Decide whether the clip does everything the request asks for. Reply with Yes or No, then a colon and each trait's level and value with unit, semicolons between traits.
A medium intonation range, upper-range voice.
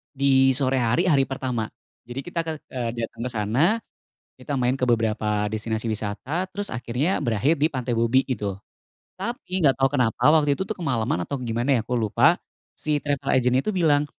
No: average, 4.1 semitones; low, 130 Hz